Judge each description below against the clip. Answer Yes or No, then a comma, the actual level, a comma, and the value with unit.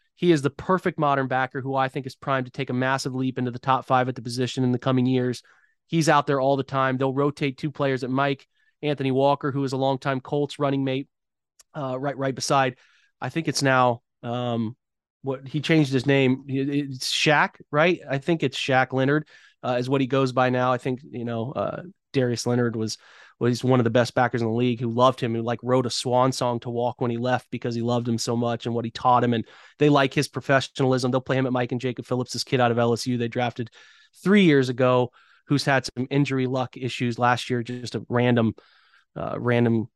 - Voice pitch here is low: Yes, low, 130 Hz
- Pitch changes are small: Yes, narrow, 2.1 semitones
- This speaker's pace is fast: Yes, fast, 235 wpm